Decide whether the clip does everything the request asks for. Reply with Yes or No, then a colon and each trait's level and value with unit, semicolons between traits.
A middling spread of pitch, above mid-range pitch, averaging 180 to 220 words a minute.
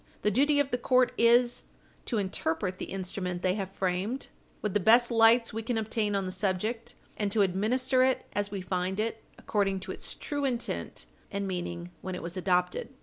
Yes: average, 4.1 semitones; high, 205 Hz; average, 195 wpm